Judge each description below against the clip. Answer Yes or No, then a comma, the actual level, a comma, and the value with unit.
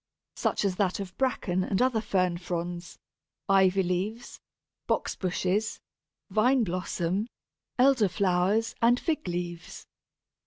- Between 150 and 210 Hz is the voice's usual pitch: Yes, high, 190 Hz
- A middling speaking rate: No, slow, 115 wpm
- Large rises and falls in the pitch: No, average, 3.8 semitones